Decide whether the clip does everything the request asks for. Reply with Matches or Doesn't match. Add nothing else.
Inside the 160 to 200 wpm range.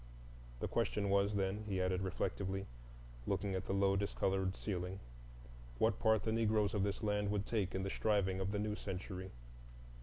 Matches